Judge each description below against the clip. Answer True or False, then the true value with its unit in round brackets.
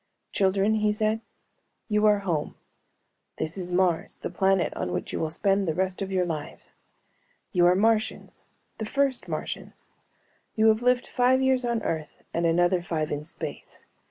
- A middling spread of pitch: True (4.0 semitones)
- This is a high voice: True (195 Hz)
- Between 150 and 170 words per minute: True (165 wpm)